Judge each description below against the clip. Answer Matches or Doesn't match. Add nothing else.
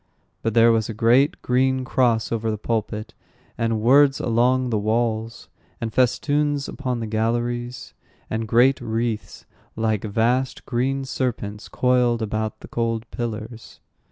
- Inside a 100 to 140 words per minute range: Matches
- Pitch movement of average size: Doesn't match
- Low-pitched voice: Matches